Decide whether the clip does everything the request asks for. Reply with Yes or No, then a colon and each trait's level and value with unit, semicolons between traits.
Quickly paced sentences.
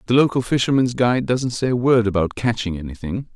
No: average, 195 wpm